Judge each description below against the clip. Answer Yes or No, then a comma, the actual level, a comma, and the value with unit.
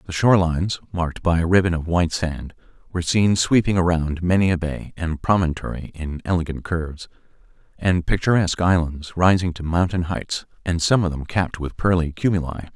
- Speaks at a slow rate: No, average, 170 wpm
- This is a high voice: No, very low, 85 Hz